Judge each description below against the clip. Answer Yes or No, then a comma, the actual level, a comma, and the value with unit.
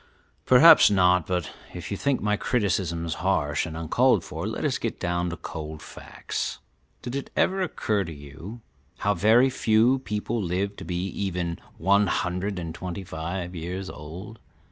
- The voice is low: Yes, very low, 95 Hz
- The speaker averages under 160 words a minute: No, average, 165 wpm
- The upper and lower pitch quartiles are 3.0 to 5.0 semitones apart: Yes, average, 3.6 semitones